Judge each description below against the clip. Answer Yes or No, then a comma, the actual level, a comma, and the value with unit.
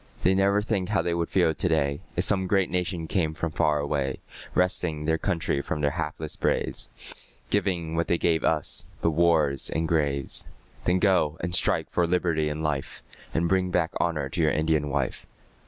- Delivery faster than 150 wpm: Yes, average, 190 wpm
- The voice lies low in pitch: Yes, very low, 80 Hz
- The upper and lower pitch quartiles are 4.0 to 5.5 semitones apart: No, average, 2.9 semitones